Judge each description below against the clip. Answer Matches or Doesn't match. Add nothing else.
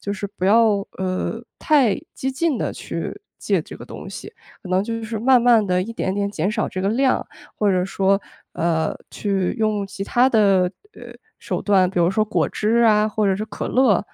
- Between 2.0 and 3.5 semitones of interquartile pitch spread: Matches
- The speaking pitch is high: Matches